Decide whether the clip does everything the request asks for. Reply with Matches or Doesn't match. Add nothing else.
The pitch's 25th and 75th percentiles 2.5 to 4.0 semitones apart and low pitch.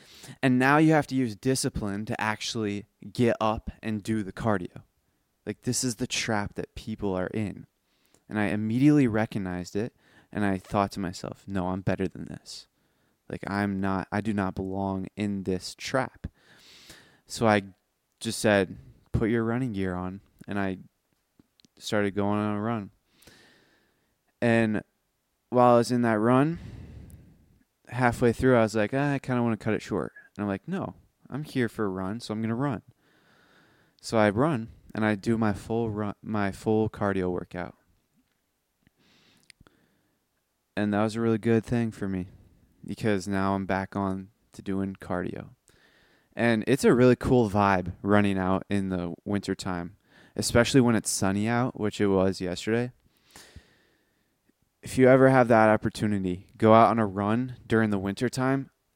Matches